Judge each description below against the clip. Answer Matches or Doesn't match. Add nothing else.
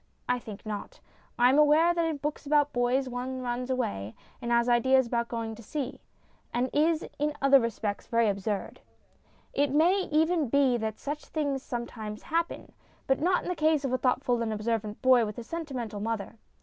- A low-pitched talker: Doesn't match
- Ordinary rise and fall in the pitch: Matches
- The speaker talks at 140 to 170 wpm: Doesn't match